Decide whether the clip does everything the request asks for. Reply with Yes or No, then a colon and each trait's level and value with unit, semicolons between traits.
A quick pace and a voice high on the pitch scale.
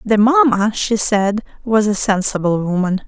No: average, 155 wpm; high, 210 Hz